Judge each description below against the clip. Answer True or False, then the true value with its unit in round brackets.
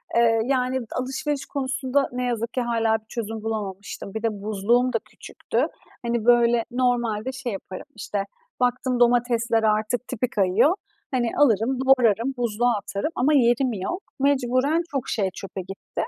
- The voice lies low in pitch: False (240 Hz)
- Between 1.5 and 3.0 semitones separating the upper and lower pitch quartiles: True (2.7 semitones)